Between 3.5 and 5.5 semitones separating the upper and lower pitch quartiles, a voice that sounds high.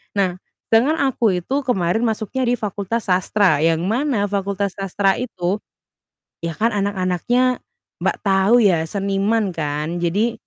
Yes: average, 3.9 semitones; high, 200 Hz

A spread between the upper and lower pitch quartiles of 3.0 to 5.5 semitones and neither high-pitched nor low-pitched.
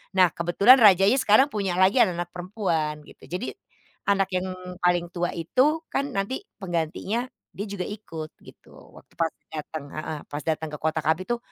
Yes: average, 4.1 semitones; medium, 180 Hz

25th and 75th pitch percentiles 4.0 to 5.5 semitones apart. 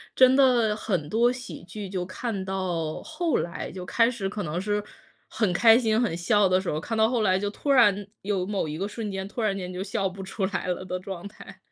No: average, 3.3 semitones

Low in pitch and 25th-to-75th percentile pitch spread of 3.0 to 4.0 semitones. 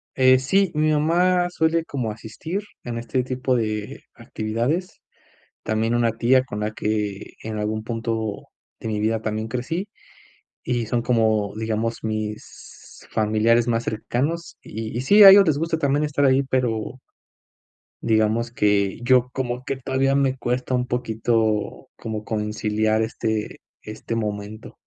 Yes: low, 115 Hz; average, 3.4 semitones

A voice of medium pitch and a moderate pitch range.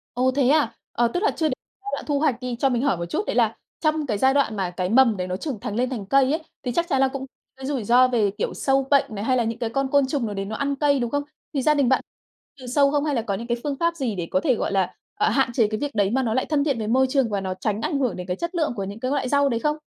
No: very high, 255 Hz; average, 4.3 semitones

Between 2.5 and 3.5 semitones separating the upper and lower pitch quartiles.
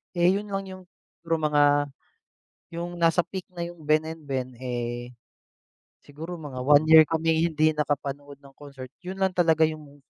Yes: average, 3.1 semitones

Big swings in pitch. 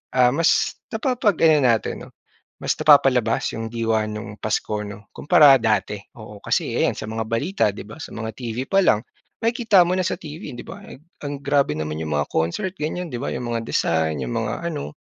Yes: wide, 6.5 semitones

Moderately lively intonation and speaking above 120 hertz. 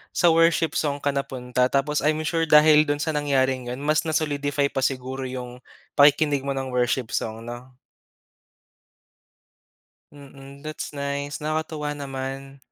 No: narrow, 2.2 semitones; medium, 140 Hz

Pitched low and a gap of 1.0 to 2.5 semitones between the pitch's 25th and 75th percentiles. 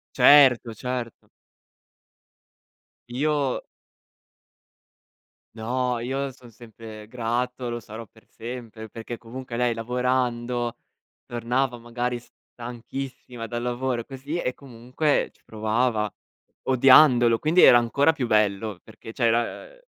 Yes: low, 120 Hz; narrow, 1.9 semitones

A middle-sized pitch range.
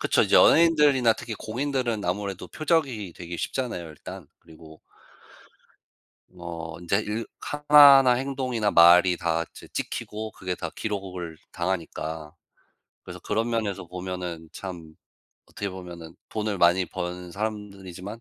Yes: average, 4.9 semitones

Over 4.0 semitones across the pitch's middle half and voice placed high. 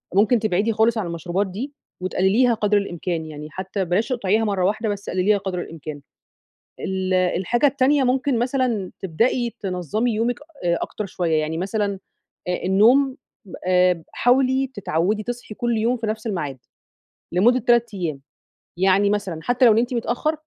Yes: average, 4.6 semitones; high, 205 Hz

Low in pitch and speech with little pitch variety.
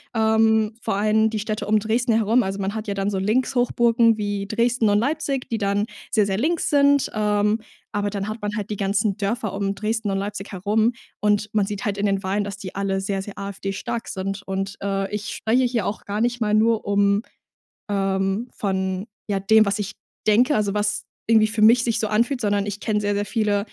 No: high, 210 Hz; narrow, 2.0 semitones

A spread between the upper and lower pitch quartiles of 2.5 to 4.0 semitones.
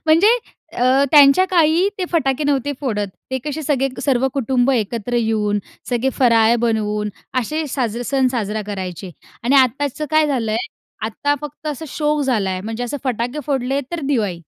No: average, 4.6 semitones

